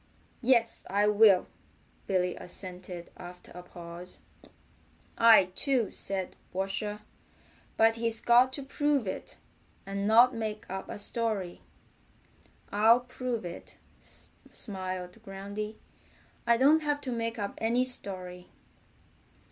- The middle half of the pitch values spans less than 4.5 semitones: Yes, average, 4.0 semitones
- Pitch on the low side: No, high, 210 Hz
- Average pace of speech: No, slow, 115 wpm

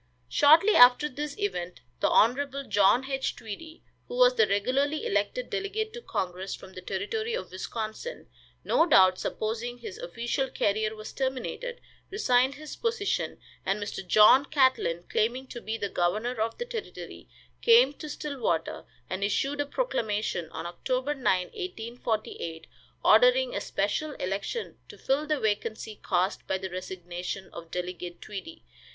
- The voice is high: Yes, high, 240 Hz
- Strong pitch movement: Yes, wide, 7.7 semitones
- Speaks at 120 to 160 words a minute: Yes, average, 145 wpm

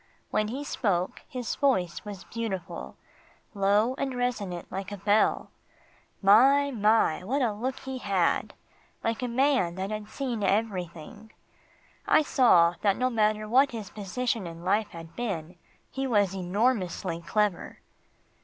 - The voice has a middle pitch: No, high, 210 Hz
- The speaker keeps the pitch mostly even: No, average, 4.7 semitones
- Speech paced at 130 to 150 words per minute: Yes, average, 140 wpm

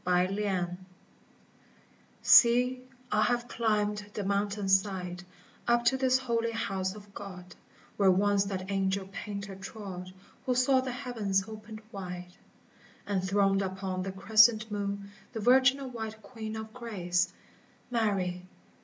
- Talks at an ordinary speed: No, slow, 130 wpm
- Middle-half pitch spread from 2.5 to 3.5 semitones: Yes, average, 3.1 semitones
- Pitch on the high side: Yes, high, 205 Hz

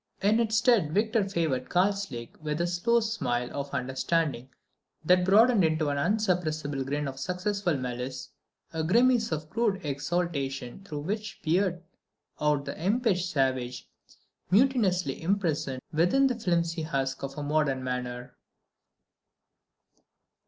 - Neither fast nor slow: No, slow, 125 wpm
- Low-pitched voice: No, medium, 165 Hz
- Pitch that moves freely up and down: Yes, wide, 6.4 semitones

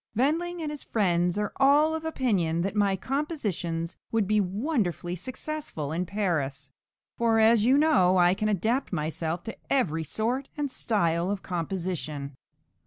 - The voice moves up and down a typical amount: No, wide, 7.2 semitones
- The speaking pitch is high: Yes, high, 200 Hz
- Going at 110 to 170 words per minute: Yes, average, 150 wpm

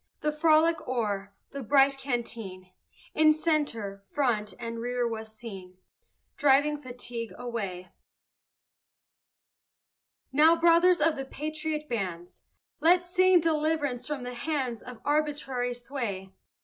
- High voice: Yes, very high, 255 Hz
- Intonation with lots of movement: No, average, 4.9 semitones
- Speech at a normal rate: No, slow, 110 wpm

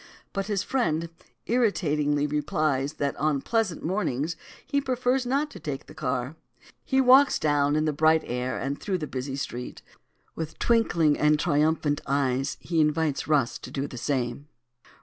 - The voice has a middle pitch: Yes, medium, 150 Hz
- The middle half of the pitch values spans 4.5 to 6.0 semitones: Yes, average, 5.2 semitones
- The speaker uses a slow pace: No, average, 160 wpm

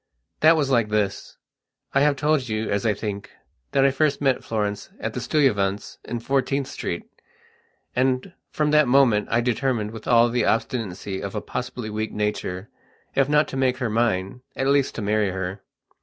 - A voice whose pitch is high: No, low, 120 Hz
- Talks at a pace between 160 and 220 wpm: Yes, average, 180 wpm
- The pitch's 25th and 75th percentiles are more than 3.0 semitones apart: Yes, average, 4.5 semitones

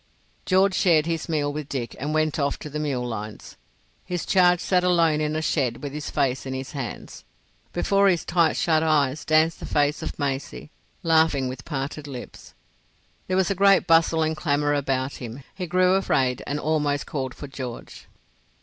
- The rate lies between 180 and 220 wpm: Yes, average, 185 wpm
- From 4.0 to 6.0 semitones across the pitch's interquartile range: No, average, 3.4 semitones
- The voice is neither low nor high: Yes, medium, 150 Hz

